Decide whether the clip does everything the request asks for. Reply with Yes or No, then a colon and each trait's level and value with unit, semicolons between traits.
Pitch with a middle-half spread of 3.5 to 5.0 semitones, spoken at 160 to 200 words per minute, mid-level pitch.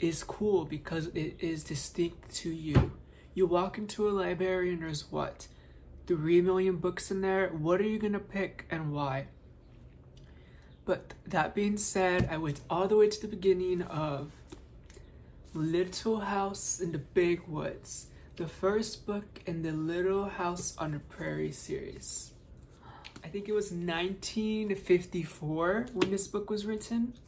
No: average, 4.0 semitones; average, 150 wpm; medium, 180 Hz